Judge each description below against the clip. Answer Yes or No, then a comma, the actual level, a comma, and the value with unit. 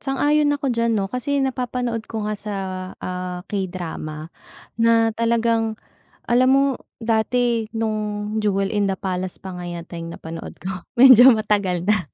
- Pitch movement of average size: Yes, average, 4.0 semitones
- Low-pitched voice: No, high, 215 Hz